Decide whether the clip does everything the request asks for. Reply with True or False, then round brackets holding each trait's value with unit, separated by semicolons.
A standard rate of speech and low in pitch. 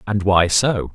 True (190 wpm; 100 Hz)